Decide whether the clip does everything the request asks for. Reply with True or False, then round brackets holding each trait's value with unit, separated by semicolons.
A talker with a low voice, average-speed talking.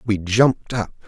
True (110 Hz; 165 wpm)